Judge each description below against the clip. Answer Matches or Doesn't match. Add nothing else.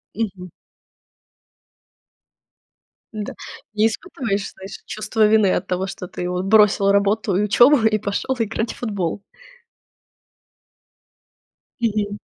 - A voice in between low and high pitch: Doesn't match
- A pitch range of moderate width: Doesn't match